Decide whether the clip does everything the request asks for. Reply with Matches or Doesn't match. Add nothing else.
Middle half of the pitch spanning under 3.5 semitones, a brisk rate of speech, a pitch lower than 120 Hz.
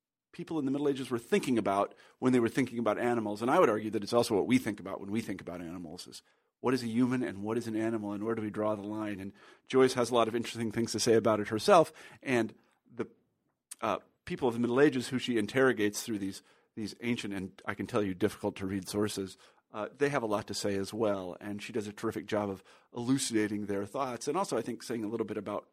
Matches